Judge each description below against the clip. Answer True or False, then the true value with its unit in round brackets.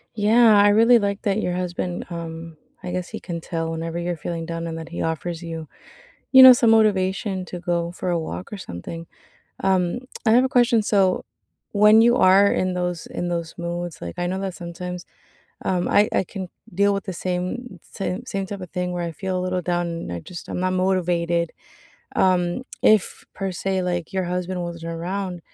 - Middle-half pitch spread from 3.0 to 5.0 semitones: False (2.4 semitones)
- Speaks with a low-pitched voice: False (180 Hz)